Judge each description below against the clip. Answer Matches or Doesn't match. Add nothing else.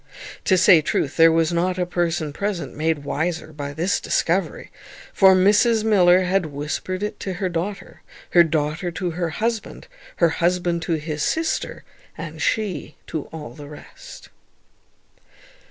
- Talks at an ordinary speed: Matches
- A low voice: Doesn't match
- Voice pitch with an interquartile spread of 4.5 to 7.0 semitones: Doesn't match